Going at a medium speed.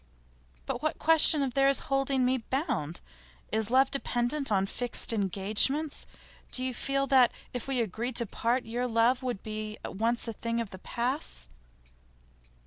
Yes: average, 165 wpm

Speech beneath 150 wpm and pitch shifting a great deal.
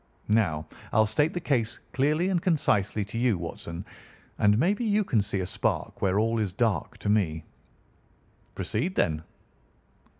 No: average, 155 wpm; wide, 7.2 semitones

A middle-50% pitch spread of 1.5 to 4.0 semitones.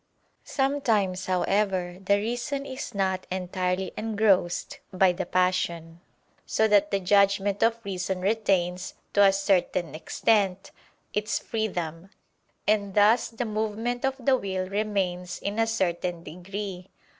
Yes: average, 2.9 semitones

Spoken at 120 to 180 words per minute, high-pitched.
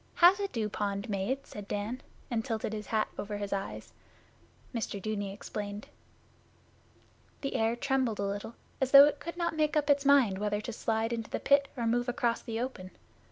No: average, 190 wpm; high, 225 Hz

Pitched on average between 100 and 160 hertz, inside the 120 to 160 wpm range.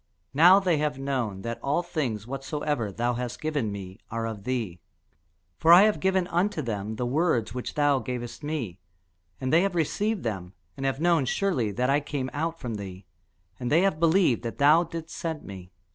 No: low, 135 Hz; average, 190 wpm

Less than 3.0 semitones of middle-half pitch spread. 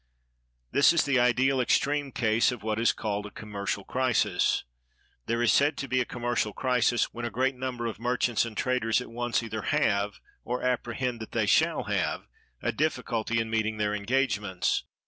Yes: narrow, 2.6 semitones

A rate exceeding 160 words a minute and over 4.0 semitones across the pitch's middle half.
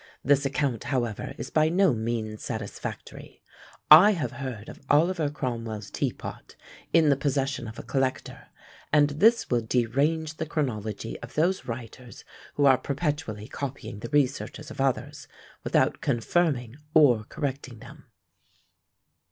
No: slow, 135 wpm; average, 4.4 semitones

